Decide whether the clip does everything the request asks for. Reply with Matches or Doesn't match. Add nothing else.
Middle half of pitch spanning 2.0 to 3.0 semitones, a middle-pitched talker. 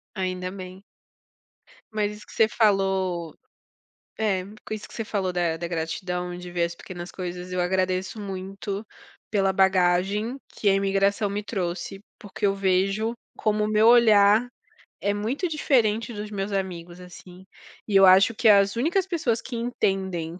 Doesn't match